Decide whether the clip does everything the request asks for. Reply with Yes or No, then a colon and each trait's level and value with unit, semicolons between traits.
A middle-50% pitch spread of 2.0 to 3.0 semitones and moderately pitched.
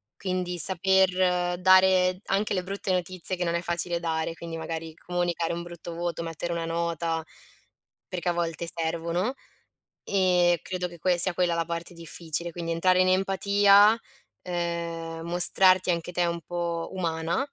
No: narrow, 1.6 semitones; medium, 175 Hz